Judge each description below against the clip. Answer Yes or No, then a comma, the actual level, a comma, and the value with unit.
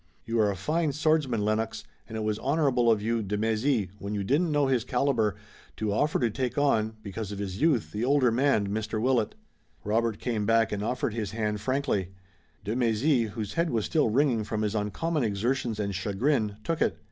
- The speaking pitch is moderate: No, low, 115 Hz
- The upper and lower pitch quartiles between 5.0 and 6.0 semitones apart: No, average, 4.1 semitones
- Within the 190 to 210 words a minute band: Yes, average, 200 wpm